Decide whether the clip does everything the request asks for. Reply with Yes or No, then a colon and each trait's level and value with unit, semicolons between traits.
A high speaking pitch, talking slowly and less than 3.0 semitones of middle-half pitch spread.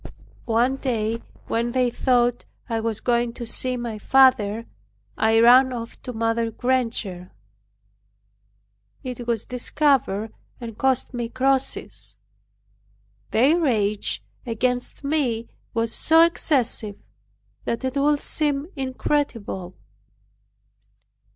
Yes: high, 240 Hz; slow, 105 wpm; narrow, 2.6 semitones